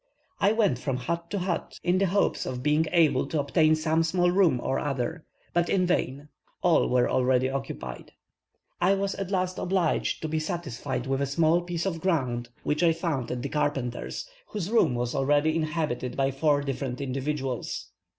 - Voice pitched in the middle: Yes, medium, 155 Hz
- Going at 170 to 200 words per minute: Yes, average, 180 wpm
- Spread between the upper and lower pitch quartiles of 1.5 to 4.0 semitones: No, average, 4.6 semitones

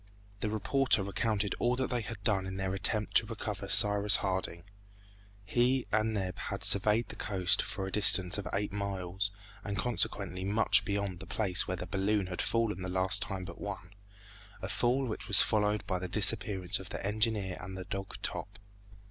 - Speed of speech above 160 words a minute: Yes, average, 185 wpm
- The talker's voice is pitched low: Yes, low, 100 Hz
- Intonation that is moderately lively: No, narrow, 2.3 semitones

